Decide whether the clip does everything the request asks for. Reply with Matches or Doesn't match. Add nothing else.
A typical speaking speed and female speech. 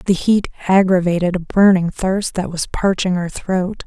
Matches